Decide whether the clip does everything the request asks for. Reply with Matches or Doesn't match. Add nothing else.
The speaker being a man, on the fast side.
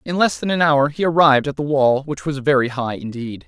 Matches